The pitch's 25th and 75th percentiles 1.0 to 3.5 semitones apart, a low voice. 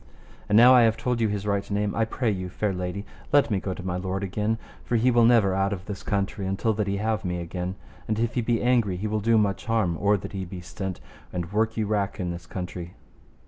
Yes: average, 3.0 semitones; low, 100 Hz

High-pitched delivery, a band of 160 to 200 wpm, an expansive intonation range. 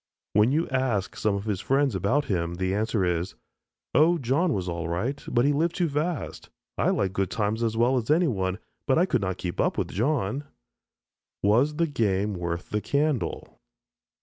No: low, 115 Hz; average, 185 wpm; wide, 7.0 semitones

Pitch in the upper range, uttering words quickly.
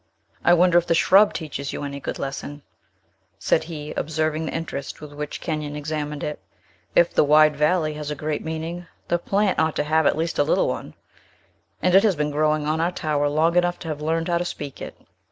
No: medium, 155 Hz; fast, 215 wpm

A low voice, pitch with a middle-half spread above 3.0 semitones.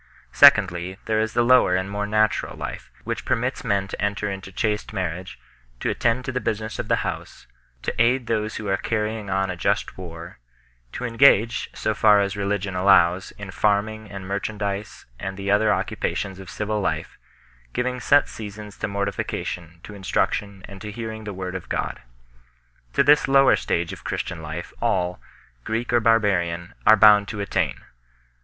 No: low, 100 Hz; narrow, 2.5 semitones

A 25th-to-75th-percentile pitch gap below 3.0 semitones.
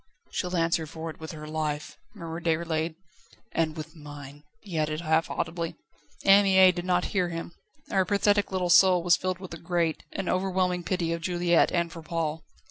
Yes: narrow, 2.4 semitones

